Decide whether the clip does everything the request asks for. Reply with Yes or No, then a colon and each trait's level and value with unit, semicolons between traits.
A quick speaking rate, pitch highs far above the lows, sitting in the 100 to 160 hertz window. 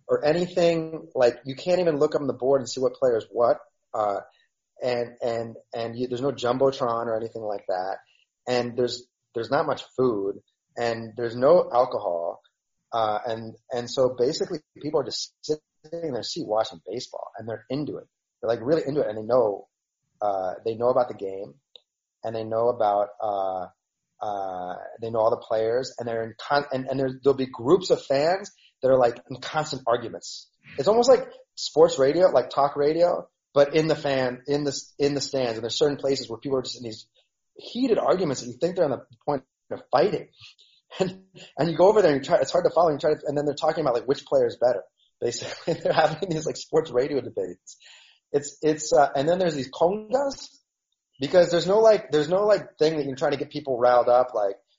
Yes: fast, 215 wpm; wide, 5.9 semitones; medium, 140 Hz